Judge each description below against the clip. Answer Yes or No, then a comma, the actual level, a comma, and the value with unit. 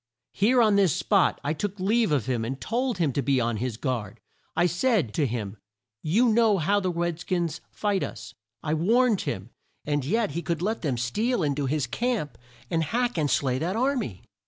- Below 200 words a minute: No, fast, 205 wpm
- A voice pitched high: No, medium, 170 Hz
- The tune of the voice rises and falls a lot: Yes, wide, 8.0 semitones